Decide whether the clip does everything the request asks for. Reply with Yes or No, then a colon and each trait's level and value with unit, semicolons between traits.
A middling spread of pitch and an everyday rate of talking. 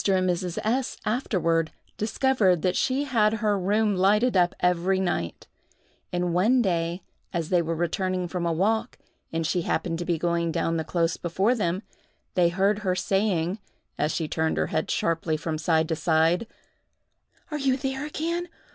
Yes: average, 4.1 semitones; average, 170 wpm